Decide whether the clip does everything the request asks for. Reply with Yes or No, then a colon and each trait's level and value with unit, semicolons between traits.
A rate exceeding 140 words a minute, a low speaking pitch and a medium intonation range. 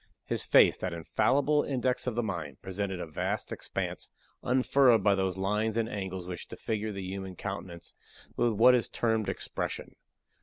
Yes: average, 160 wpm; low, 100 Hz; average, 4.1 semitones